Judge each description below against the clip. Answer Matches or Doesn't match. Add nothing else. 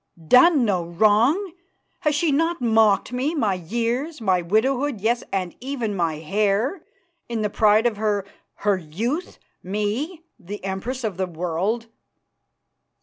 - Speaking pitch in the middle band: Doesn't match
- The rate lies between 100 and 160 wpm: Matches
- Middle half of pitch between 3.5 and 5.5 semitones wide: Matches